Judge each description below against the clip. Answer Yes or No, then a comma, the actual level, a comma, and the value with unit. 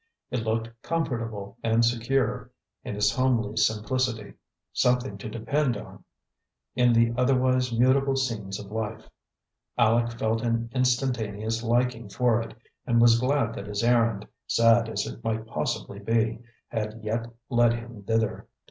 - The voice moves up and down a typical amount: No, narrow, 2.0 semitones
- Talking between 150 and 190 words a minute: No, average, 140 wpm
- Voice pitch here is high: No, low, 115 Hz